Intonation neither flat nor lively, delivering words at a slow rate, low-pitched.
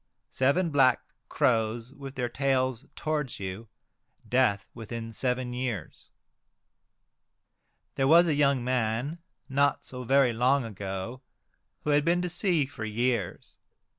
Yes: average, 3.5 semitones; slow, 125 wpm; low, 130 Hz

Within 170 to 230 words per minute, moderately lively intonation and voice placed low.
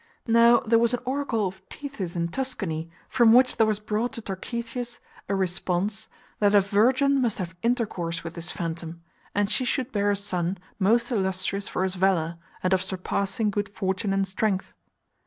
No: average, 180 wpm; average, 3.9 semitones; high, 200 Hz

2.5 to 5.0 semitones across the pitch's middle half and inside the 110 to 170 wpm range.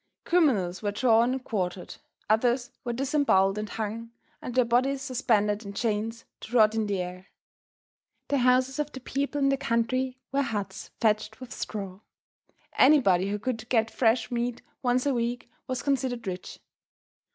Yes: average, 3.5 semitones; average, 160 wpm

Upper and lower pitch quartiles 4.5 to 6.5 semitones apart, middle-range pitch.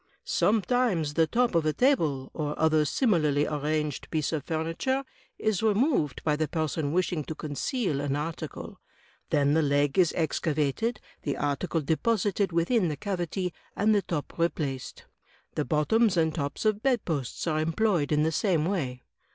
Yes: average, 5.1 semitones; medium, 160 Hz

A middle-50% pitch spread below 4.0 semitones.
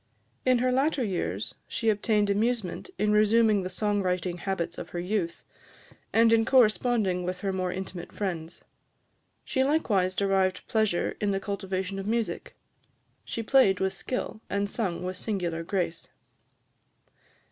Yes: average, 3.4 semitones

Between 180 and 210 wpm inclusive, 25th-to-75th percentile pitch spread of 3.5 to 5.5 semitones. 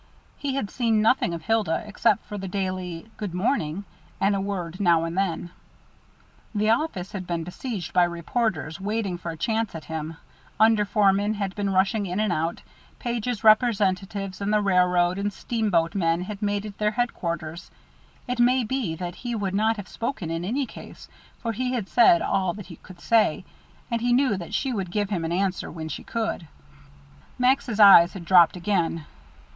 Yes: average, 185 wpm; average, 4.0 semitones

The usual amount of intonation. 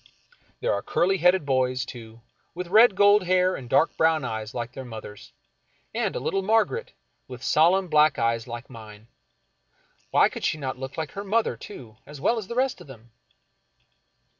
No: wide, 8.2 semitones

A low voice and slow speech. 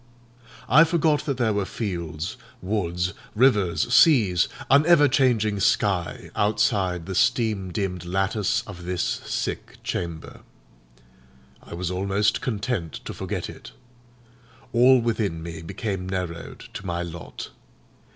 Yes: very low, 95 Hz; slow, 120 wpm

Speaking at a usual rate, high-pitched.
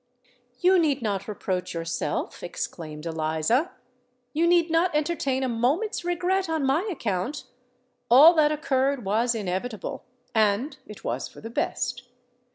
No: slow, 130 wpm; very high, 255 Hz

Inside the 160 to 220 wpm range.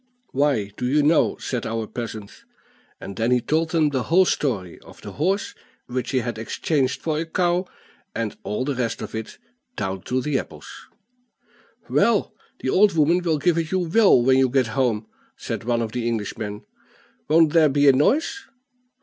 Yes: average, 185 wpm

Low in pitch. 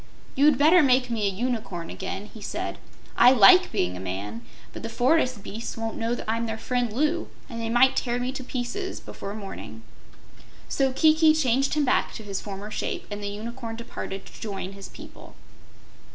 No: high, 230 Hz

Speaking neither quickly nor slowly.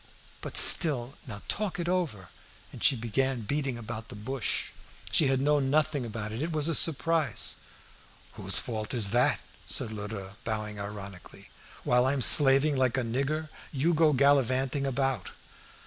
Yes: average, 155 wpm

